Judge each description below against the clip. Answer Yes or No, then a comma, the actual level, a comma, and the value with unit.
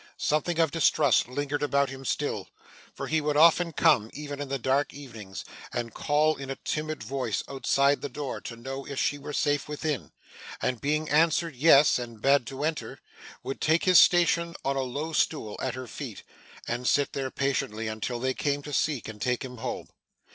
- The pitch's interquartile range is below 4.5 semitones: Yes, average, 3.0 semitones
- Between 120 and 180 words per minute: No, average, 190 wpm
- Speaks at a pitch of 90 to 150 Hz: Yes, medium, 140 Hz